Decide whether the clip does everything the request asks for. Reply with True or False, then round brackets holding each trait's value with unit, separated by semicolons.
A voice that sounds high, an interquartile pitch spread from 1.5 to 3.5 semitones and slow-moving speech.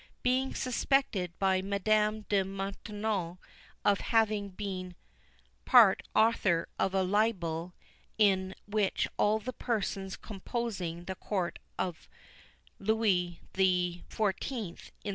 True (195 Hz; 2.8 semitones; 100 wpm)